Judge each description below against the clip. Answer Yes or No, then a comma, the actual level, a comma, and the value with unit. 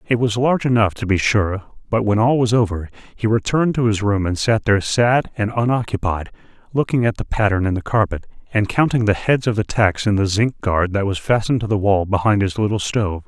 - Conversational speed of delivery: No, fast, 230 wpm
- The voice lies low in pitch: Yes, low, 110 Hz